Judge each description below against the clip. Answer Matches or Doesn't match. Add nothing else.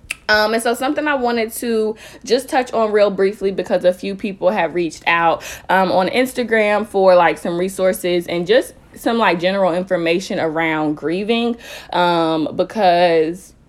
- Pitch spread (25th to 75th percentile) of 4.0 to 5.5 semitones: Matches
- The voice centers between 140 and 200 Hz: Matches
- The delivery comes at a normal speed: Matches